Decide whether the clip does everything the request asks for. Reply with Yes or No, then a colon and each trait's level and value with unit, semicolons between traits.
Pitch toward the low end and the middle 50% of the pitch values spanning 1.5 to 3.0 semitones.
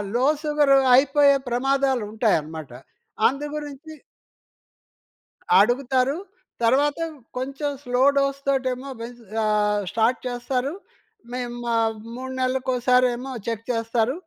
No: very high, 255 Hz; narrow, 2.5 semitones